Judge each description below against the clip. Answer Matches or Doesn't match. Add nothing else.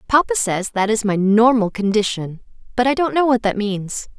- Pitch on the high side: Matches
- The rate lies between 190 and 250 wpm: Matches